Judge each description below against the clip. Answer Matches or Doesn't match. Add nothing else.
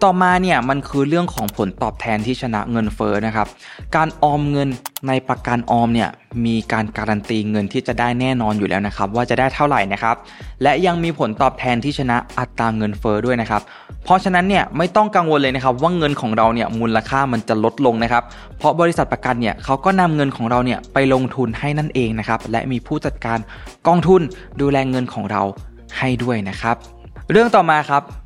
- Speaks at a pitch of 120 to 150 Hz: Matches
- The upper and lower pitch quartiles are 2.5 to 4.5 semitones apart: Matches